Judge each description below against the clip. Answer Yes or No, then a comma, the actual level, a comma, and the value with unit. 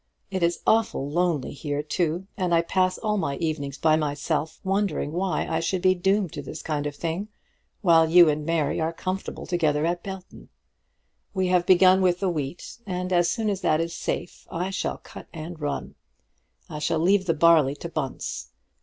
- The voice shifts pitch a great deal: No, average, 3.2 semitones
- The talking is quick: No, average, 190 wpm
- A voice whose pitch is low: No, medium, 170 Hz